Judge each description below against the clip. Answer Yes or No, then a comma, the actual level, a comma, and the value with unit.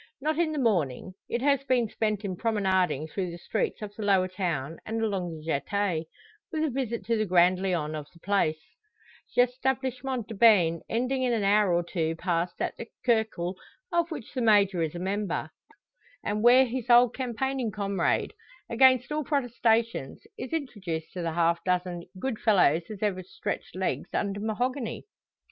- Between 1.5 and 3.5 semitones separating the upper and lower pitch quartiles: No, wide, 5.6 semitones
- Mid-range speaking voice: No, high, 210 Hz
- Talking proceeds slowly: No, average, 175 wpm